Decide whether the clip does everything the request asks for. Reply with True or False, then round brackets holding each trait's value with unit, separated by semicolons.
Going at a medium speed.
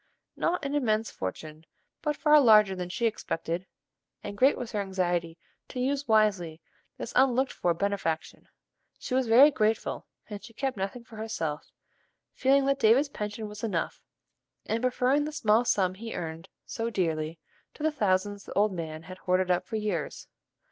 True (170 wpm)